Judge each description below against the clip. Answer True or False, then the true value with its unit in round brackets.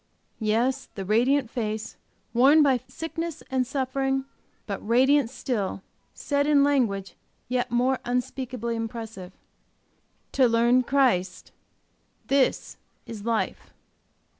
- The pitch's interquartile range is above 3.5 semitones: False (3.0 semitones)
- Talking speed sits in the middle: False (105 wpm)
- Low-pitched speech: False (250 Hz)